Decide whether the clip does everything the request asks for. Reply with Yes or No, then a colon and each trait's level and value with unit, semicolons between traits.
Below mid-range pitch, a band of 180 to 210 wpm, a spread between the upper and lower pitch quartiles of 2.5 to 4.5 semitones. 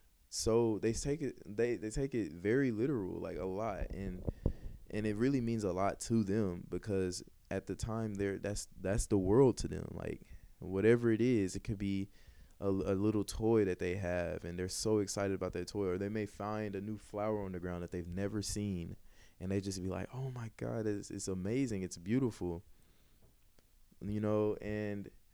Yes: low, 100 Hz; average, 200 wpm; average, 2.8 semitones